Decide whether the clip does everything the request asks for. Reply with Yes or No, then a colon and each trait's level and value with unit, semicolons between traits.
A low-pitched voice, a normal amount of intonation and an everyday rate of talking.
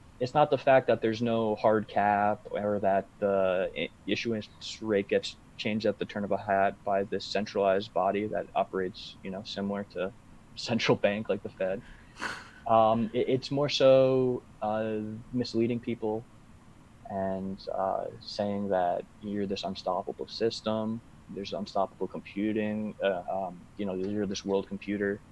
No: low, 105 Hz; narrow, 2.3 semitones; average, 150 wpm